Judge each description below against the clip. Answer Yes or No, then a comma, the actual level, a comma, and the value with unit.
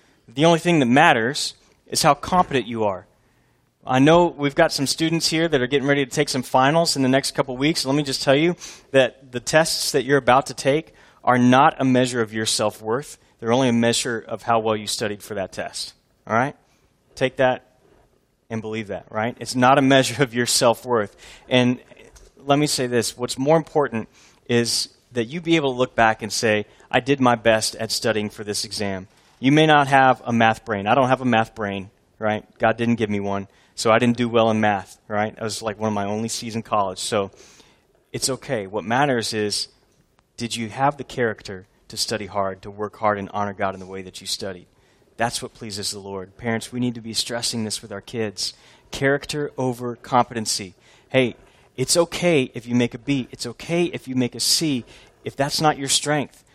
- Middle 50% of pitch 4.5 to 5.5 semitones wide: No, average, 3.8 semitones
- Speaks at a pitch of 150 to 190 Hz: No, low, 120 Hz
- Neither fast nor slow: No, fast, 220 wpm